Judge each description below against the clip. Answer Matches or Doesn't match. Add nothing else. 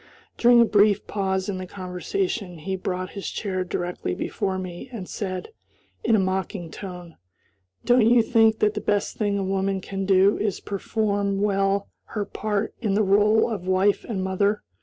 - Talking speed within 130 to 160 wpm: Doesn't match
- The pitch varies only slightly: Matches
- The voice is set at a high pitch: Matches